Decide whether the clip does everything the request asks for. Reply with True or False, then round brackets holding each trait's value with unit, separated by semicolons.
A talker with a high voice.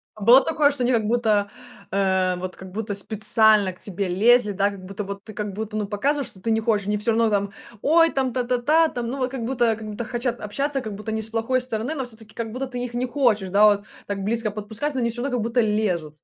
True (220 Hz)